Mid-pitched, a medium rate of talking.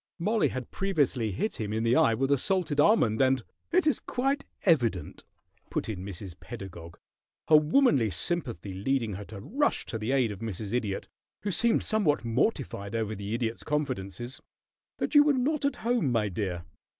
No: low, 125 Hz; average, 180 wpm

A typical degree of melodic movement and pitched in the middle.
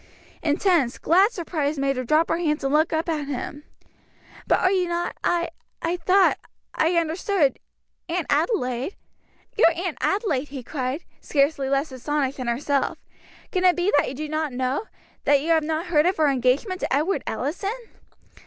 No: average, 4.0 semitones; very high, 310 Hz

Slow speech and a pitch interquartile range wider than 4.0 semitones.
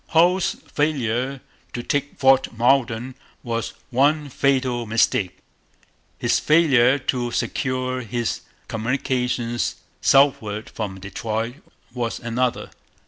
No: slow, 95 wpm; average, 3.0 semitones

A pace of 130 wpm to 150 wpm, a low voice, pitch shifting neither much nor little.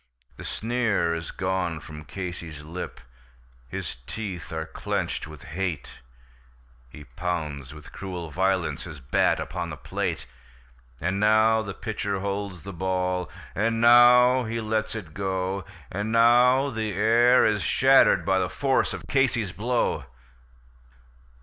Yes: slow, 135 wpm; very low, 95 Hz; average, 4.7 semitones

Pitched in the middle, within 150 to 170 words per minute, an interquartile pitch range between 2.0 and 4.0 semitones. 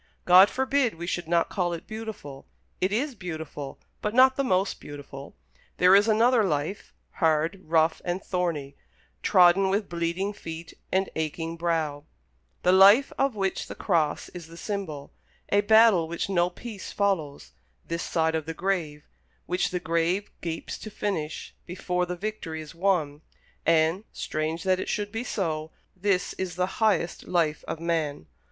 Yes: medium, 175 Hz; average, 160 wpm; average, 3.7 semitones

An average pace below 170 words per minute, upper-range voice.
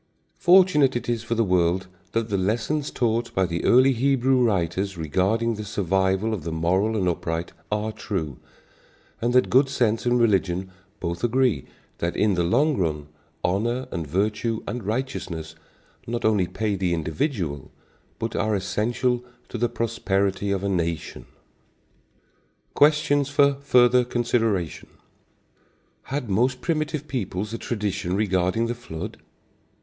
No: average, 140 wpm; low, 110 Hz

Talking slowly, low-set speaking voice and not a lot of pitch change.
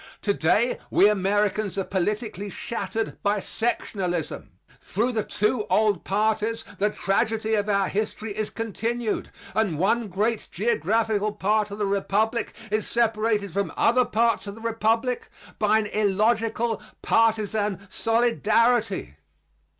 No: slow, 125 wpm; high, 215 Hz; narrow, 1.9 semitones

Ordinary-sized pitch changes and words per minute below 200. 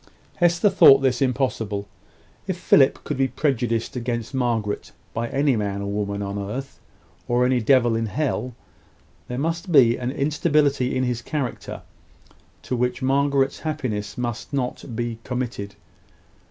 Yes: average, 3.3 semitones; average, 140 wpm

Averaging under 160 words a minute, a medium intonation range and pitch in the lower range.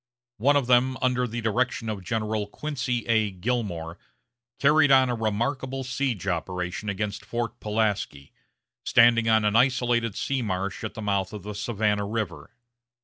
Yes: average, 150 wpm; average, 3.4 semitones; low, 110 Hz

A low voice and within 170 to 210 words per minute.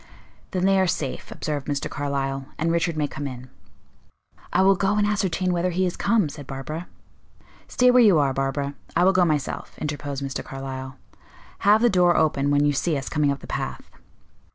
No: medium, 155 Hz; average, 195 wpm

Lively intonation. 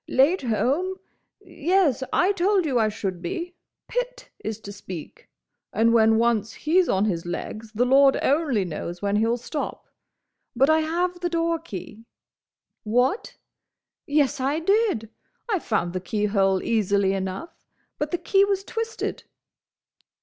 Yes: wide, 8.6 semitones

